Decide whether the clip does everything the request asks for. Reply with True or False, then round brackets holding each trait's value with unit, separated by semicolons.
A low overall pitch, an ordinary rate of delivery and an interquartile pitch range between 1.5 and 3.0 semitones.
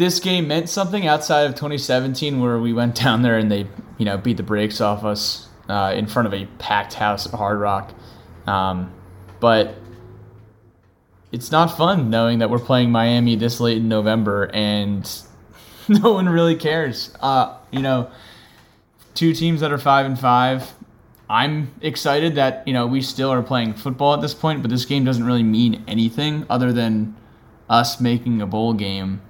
False (120 Hz; 180 wpm; 4.2 semitones)